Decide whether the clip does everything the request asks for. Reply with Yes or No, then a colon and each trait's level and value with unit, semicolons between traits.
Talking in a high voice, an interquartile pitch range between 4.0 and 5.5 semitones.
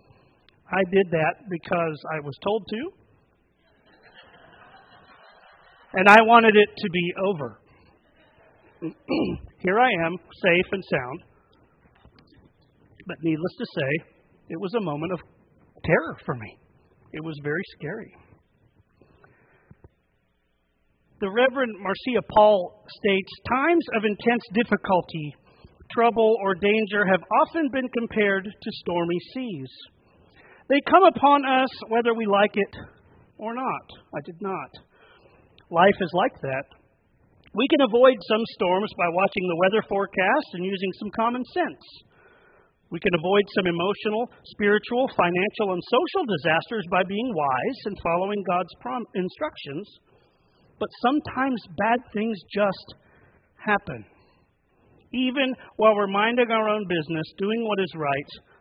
Yes: high, 205 Hz; average, 4.6 semitones